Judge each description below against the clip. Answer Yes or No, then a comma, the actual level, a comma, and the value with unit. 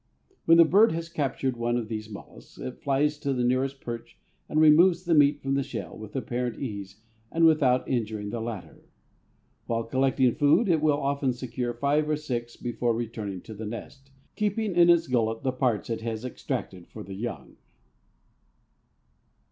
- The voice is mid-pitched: No, low, 130 Hz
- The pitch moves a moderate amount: Yes, average, 4.4 semitones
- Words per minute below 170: No, average, 175 wpm